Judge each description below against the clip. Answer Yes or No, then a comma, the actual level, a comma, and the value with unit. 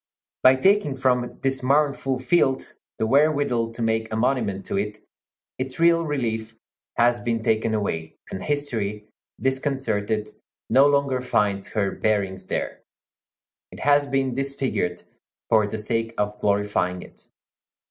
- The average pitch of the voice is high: No, low, 120 Hz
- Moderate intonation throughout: Yes, average, 4.2 semitones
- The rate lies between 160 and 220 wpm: No, slow, 135 wpm